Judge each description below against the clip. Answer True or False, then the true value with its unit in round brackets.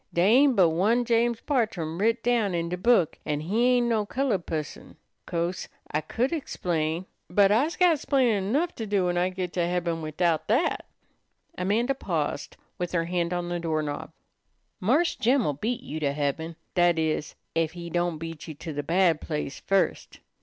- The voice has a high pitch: False (180 Hz)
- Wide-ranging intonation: True (5.9 semitones)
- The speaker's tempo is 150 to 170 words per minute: False (180 wpm)